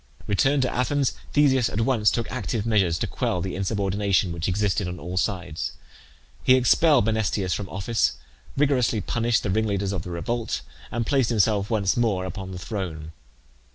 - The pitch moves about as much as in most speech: Yes, average, 4.2 semitones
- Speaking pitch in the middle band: No, low, 105 Hz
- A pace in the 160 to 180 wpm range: Yes, average, 165 wpm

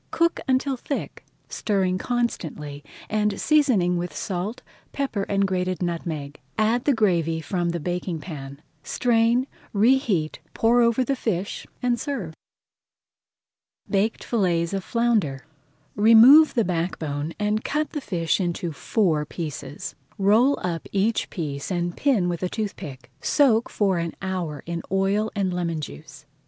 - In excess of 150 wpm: No, average, 140 wpm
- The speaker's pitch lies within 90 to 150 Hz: No, high, 190 Hz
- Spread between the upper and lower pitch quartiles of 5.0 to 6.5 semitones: Yes, wide, 5.4 semitones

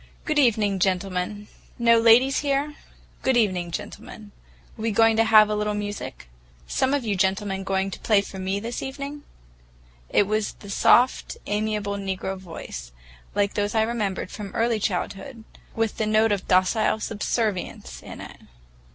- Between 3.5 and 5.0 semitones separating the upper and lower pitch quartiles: No, average, 2.8 semitones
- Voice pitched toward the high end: Yes, high, 210 Hz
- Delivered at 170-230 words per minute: No, average, 155 wpm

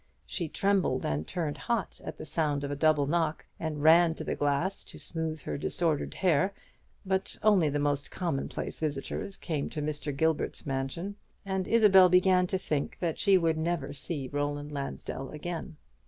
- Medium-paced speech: Yes, average, 170 wpm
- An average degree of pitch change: Yes, average, 4.0 semitones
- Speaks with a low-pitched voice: No, medium, 160 Hz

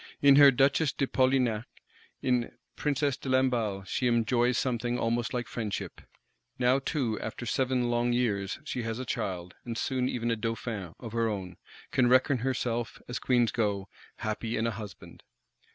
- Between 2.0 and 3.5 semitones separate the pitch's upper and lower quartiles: Yes, narrow, 2.4 semitones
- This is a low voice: Yes, low, 120 Hz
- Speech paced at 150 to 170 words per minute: Yes, average, 165 wpm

